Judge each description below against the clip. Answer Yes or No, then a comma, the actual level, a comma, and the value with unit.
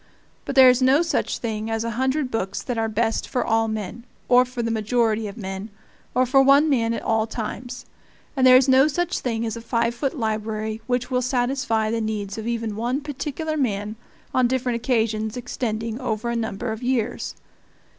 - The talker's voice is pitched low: No, high, 235 Hz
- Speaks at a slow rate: No, average, 195 wpm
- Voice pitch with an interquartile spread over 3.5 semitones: No, narrow, 2.6 semitones